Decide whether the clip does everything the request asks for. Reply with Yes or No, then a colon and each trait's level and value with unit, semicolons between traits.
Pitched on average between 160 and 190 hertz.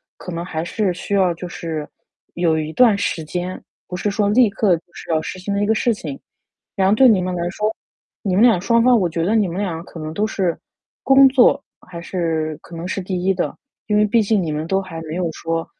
Yes: medium, 185 Hz